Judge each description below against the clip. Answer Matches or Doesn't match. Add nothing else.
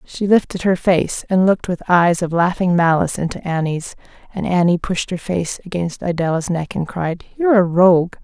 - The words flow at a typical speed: Matches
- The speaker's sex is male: Doesn't match